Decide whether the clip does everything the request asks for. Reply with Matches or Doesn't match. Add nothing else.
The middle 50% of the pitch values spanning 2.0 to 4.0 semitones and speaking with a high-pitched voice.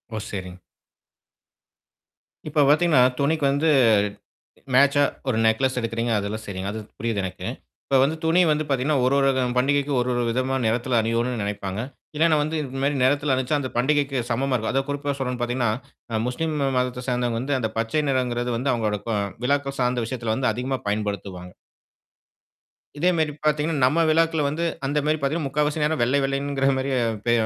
Doesn't match